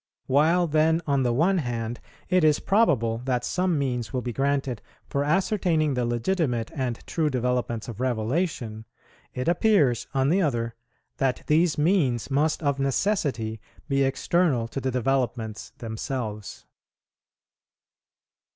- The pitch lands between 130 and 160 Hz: Yes, low, 135 Hz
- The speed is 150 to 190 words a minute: No, slow, 135 wpm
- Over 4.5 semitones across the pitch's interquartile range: Yes, average, 4.9 semitones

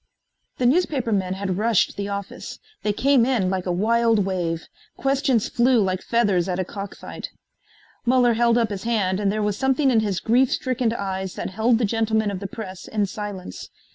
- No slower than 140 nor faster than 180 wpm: No, average, 190 wpm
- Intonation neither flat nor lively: Yes, average, 3.7 semitones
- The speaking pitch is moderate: No, high, 215 Hz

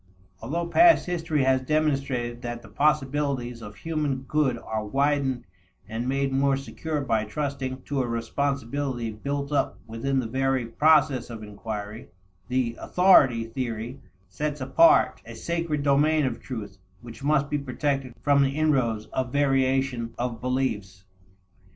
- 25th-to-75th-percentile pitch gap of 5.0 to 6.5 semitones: No, average, 3.5 semitones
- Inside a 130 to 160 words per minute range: Yes, average, 140 wpm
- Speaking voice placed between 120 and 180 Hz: Yes, low, 135 Hz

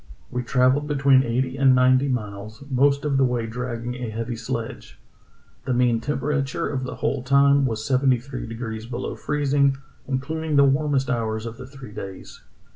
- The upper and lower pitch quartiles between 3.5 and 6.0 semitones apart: No, average, 2.9 semitones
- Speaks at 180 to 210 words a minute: No, average, 170 wpm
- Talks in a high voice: No, low, 130 Hz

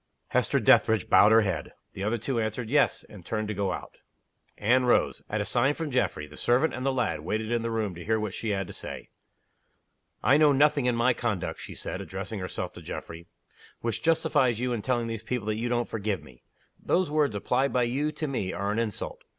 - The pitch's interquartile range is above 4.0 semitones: No, average, 3.7 semitones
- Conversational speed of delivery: No, fast, 225 wpm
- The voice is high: No, low, 115 Hz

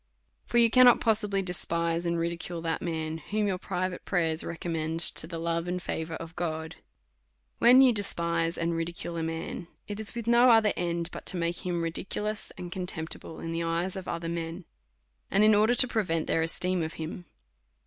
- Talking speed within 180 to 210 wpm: Yes, average, 195 wpm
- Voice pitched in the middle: Yes, medium, 170 Hz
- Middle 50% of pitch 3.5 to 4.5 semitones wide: No, average, 3.1 semitones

